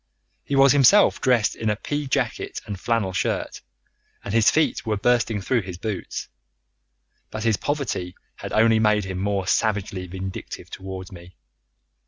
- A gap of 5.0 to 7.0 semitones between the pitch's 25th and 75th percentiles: No, average, 3.9 semitones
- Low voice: Yes, low, 105 Hz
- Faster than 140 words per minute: Yes, average, 155 wpm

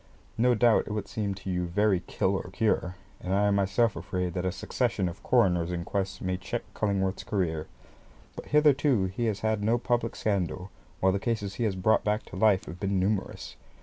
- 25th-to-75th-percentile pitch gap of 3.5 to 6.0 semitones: No, average, 2.8 semitones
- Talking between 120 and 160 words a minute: No, fast, 205 wpm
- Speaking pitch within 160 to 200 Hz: No, low, 100 Hz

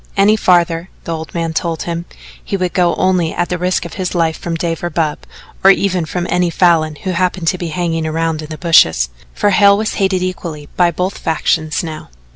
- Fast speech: Yes, fast, 215 wpm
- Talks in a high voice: No, medium, 170 Hz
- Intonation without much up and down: Yes, narrow, 2.1 semitones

